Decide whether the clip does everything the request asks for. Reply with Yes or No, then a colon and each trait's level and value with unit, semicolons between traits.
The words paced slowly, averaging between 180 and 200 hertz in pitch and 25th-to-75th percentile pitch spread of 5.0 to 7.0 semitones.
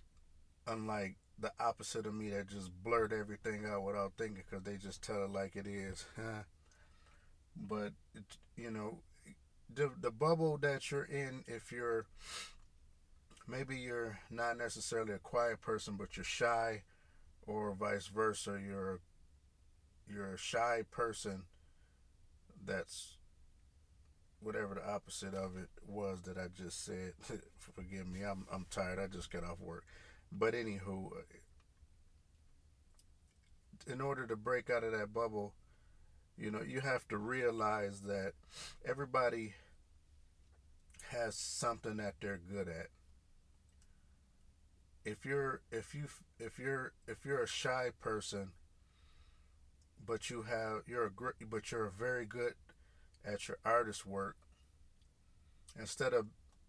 No: slow, 130 wpm; low, 100 Hz; wide, 5.6 semitones